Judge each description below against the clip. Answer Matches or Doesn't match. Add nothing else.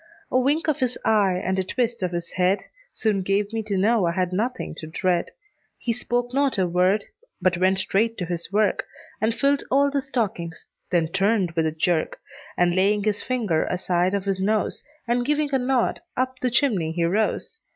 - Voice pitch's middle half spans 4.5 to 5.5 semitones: Matches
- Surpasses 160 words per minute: Matches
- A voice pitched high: Matches